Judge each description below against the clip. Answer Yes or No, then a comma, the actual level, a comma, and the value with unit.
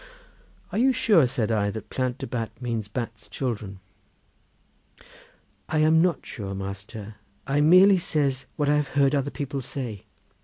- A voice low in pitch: Yes, low, 130 Hz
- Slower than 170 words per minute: Yes, average, 155 wpm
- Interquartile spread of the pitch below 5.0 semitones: No, wide, 5.4 semitones